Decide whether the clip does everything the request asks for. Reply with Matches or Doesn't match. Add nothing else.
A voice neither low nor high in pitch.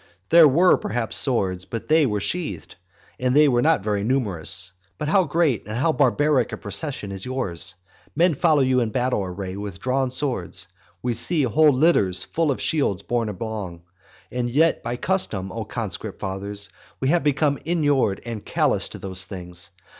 Doesn't match